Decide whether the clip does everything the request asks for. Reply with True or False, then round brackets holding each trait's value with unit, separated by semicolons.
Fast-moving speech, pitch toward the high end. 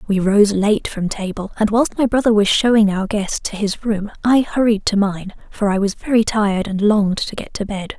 True (235 wpm; 205 Hz)